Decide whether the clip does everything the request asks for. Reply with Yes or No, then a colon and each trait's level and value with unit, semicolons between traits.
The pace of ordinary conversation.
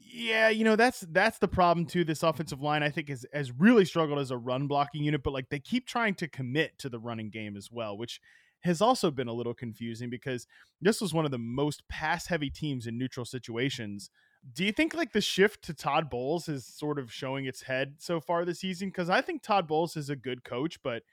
No: fast, 235 wpm